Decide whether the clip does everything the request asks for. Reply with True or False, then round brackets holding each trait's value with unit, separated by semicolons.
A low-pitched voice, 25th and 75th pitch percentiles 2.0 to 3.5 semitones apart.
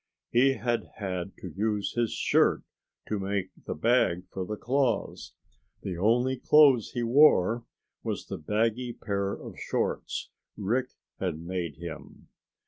False (105 Hz; 4.5 semitones)